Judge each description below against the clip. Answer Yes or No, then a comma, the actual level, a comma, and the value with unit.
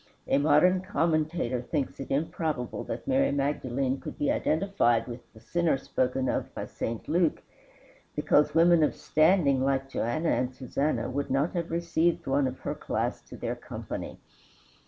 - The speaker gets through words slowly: No, average, 155 wpm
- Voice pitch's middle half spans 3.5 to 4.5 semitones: Yes, average, 4.2 semitones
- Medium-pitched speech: Yes, medium, 145 Hz